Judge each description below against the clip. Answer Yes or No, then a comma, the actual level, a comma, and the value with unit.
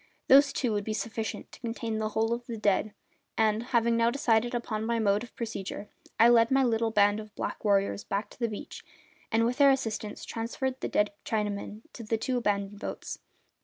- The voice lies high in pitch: Yes, high, 225 Hz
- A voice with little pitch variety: Yes, narrow, 1.9 semitones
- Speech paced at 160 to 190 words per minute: No, average, 200 wpm